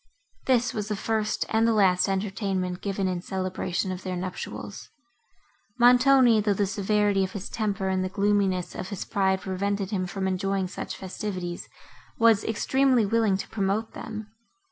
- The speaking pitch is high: Yes, high, 200 Hz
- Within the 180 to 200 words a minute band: No, average, 160 wpm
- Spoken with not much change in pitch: Yes, narrow, 2.3 semitones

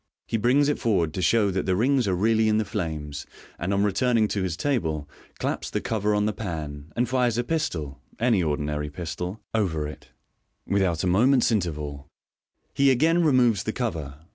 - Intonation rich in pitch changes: Yes, wide, 6.6 semitones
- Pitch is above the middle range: No, low, 100 Hz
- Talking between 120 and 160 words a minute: No, average, 190 wpm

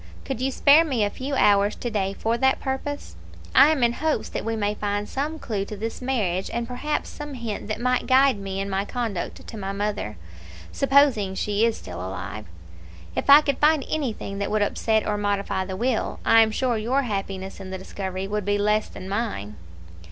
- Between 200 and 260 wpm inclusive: Yes, fast, 205 wpm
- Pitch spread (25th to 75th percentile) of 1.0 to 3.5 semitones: No, average, 4.7 semitones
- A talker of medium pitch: No, high, 215 Hz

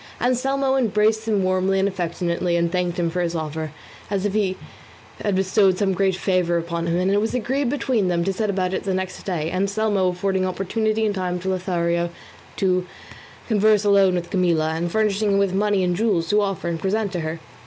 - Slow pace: No, fast, 205 wpm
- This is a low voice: No, high, 190 Hz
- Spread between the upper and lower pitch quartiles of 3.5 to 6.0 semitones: No, average, 2.9 semitones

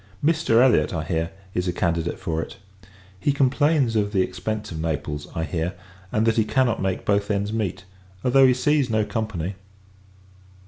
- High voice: No, low, 105 Hz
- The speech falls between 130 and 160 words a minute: No, average, 175 wpm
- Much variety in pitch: Yes, wide, 6.3 semitones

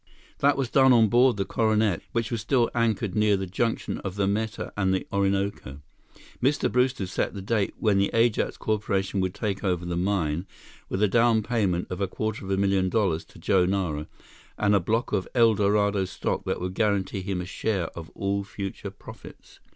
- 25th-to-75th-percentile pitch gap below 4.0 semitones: Yes, average, 2.7 semitones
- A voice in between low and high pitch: No, low, 100 Hz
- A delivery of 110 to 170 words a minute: No, average, 195 wpm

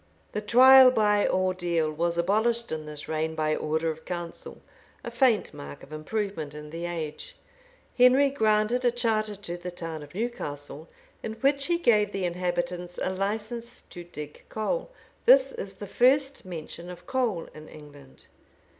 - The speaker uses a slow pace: No, average, 160 wpm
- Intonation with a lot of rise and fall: Yes, wide, 6.6 semitones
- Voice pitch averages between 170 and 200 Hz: Yes, medium, 185 Hz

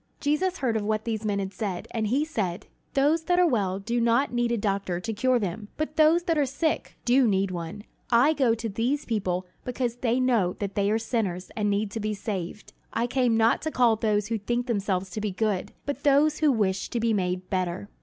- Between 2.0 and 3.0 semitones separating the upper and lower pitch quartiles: No, average, 4.1 semitones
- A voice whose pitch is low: No, high, 225 Hz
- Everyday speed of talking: No, fast, 225 wpm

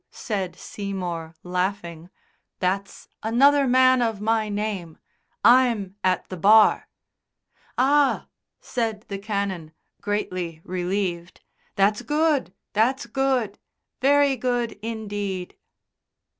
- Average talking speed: No, slow, 95 wpm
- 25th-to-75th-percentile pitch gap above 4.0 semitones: Yes, average, 4.8 semitones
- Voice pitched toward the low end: No, high, 205 Hz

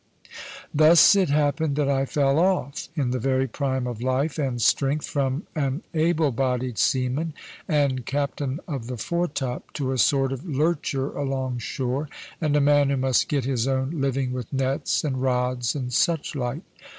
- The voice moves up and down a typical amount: No, narrow, 2.3 semitones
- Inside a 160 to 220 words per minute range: Yes, average, 165 wpm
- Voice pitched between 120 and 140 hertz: Yes, low, 135 Hz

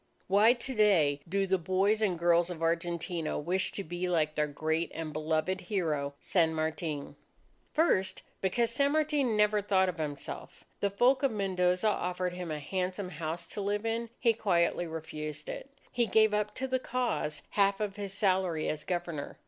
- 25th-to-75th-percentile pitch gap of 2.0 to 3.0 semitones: No, average, 4.5 semitones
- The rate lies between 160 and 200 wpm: Yes, average, 175 wpm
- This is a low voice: No, medium, 185 Hz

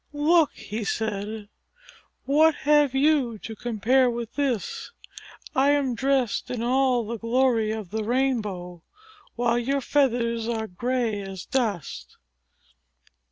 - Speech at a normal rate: No, slow, 120 wpm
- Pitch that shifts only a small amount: No, average, 3.6 semitones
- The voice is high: Yes, high, 235 Hz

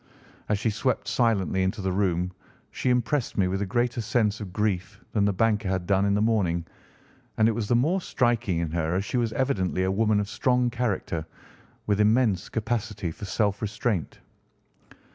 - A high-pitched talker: No, low, 105 Hz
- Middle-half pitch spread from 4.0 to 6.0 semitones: No, average, 3.6 semitones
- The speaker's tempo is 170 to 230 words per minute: Yes, average, 185 wpm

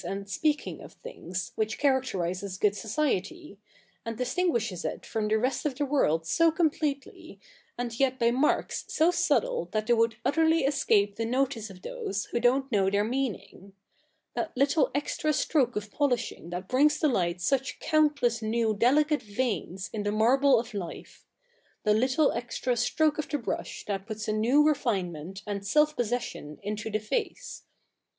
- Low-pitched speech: No, high, 240 Hz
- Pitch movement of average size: No, wide, 5.7 semitones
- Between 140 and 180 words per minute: Yes, average, 170 wpm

